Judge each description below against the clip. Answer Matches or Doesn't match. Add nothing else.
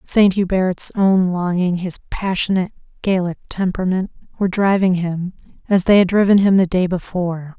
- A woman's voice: Matches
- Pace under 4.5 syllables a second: Doesn't match